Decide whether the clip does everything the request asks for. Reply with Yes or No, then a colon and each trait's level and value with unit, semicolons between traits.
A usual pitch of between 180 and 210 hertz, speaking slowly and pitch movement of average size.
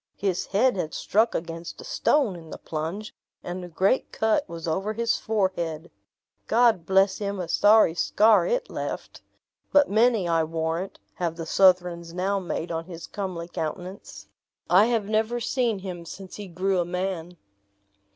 No: medium, 185 Hz; average, 160 wpm; average, 3.9 semitones